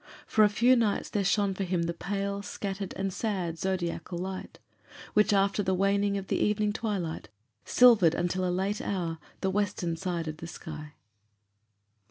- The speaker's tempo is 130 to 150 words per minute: No, average, 170 wpm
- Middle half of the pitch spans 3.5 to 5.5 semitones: No, average, 2.8 semitones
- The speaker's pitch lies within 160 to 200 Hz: Yes, high, 190 Hz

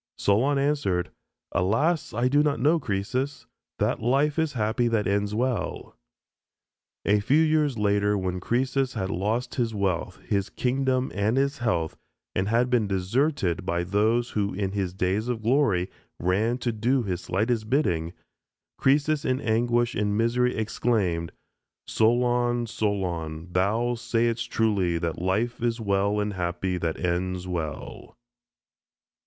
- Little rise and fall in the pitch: No, average, 4.7 semitones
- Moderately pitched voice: No, low, 110 Hz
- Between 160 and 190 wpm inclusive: No, average, 140 wpm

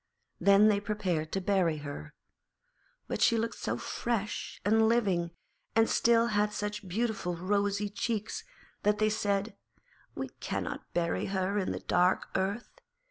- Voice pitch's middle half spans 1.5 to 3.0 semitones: Yes, narrow, 2.4 semitones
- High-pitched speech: Yes, high, 205 Hz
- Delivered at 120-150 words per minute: Yes, average, 140 wpm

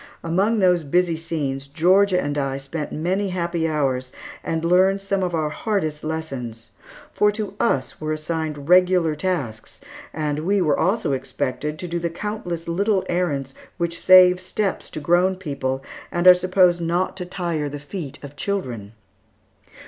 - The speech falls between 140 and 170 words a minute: Yes, average, 155 wpm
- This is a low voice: No, medium, 170 Hz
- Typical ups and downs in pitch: Yes, average, 3.9 semitones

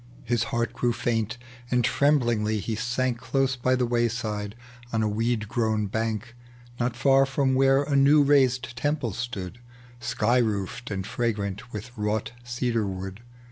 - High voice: No, low, 120 Hz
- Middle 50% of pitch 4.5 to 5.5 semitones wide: No, average, 2.9 semitones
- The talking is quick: No, average, 155 wpm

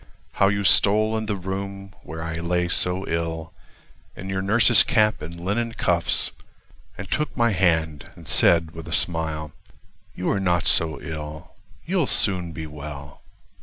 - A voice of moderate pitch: No, very low, 90 Hz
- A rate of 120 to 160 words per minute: Yes, average, 155 wpm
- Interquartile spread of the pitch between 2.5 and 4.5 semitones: Yes, average, 3.5 semitones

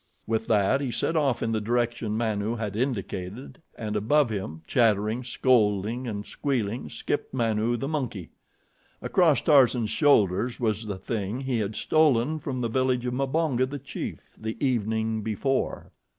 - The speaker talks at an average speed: Yes, average, 150 wpm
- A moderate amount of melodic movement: Yes, average, 3.6 semitones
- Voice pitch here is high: No, low, 115 Hz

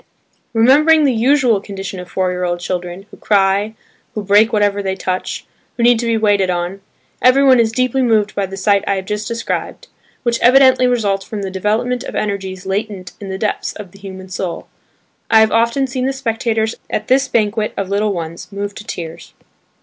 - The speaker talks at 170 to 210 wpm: Yes, average, 195 wpm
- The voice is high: Yes, high, 210 Hz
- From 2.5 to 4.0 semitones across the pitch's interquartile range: Yes, average, 3.4 semitones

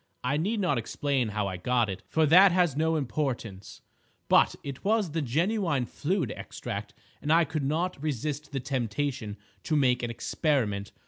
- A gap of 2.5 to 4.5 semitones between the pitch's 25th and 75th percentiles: No, average, 5.0 semitones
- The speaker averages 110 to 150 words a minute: No, average, 170 wpm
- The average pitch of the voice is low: No, medium, 145 Hz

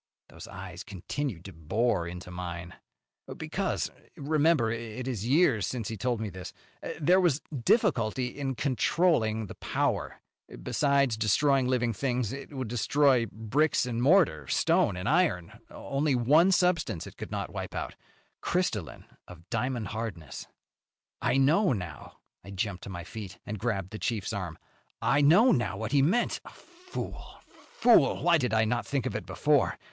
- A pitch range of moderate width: No, wide, 6.3 semitones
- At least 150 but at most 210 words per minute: Yes, average, 155 wpm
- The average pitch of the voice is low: Yes, low, 120 Hz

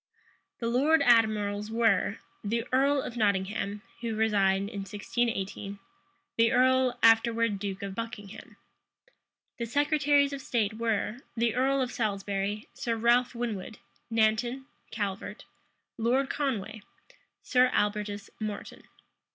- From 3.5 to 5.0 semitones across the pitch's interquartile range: No, average, 3.1 semitones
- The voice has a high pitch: Yes, high, 225 Hz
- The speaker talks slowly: Yes, slow, 115 wpm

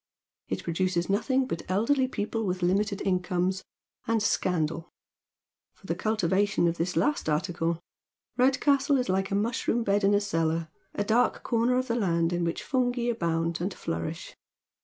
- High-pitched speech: Yes, high, 195 Hz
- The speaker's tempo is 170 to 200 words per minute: No, average, 160 wpm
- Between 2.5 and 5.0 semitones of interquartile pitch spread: No, wide, 5.4 semitones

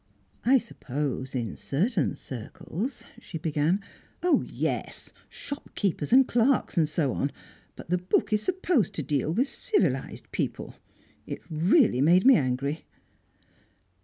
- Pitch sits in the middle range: Yes, medium, 170 Hz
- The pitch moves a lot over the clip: Yes, wide, 8.9 semitones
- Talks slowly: Yes, slow, 130 wpm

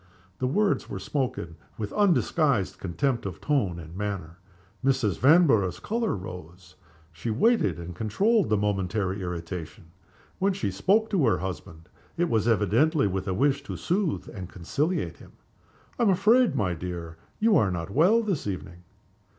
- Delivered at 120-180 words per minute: Yes, average, 155 wpm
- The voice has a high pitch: No, low, 105 Hz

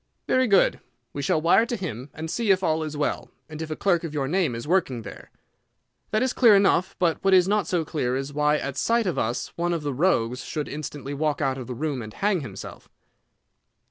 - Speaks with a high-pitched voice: No, medium, 155 Hz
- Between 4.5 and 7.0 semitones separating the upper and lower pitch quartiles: Yes, average, 5.3 semitones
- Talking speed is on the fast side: Yes, fast, 230 wpm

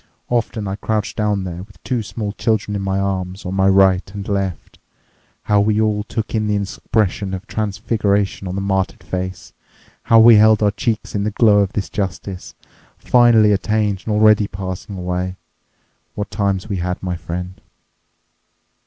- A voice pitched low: Yes, low, 100 Hz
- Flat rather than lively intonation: Yes, narrow, 2.1 semitones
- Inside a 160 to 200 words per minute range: Yes, average, 170 wpm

